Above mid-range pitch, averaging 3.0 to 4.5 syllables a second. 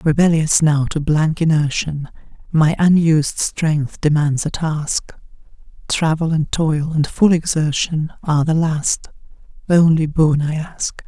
No: medium, 155 Hz; 4.0 syllables/s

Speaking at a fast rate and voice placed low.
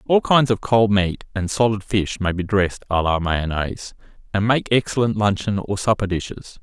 No: average, 190 wpm; low, 100 Hz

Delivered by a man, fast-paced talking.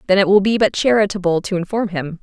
No: female; fast, 245 wpm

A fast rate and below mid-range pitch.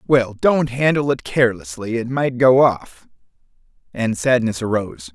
No: average, 140 wpm; low, 120 Hz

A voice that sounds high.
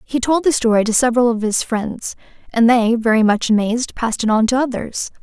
Yes: high, 235 Hz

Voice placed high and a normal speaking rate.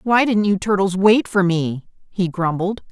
Yes: high, 195 Hz; average, 185 wpm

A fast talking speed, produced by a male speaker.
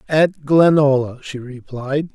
No: slow, 110 wpm; male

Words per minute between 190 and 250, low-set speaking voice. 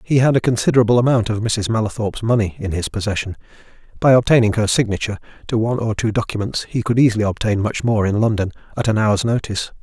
Yes: average, 200 wpm; low, 110 Hz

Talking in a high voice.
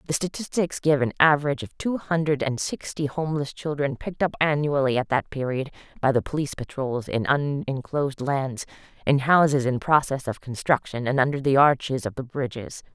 No: medium, 140 Hz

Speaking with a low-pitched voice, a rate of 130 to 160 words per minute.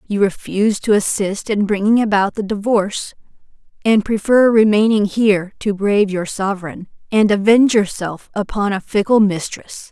No: high, 205 Hz; average, 145 wpm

